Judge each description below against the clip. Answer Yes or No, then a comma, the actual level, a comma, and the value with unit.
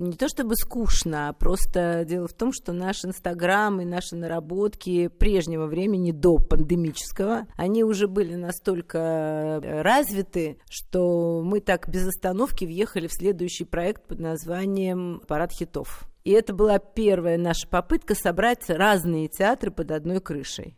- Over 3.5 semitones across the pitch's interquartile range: No, average, 3.2 semitones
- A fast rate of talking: No, average, 140 wpm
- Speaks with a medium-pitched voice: Yes, medium, 180 Hz